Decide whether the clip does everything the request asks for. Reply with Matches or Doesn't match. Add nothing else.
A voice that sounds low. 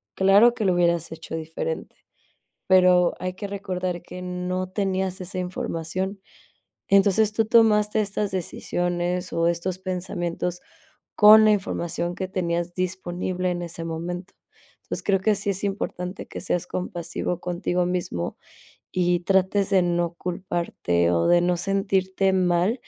Doesn't match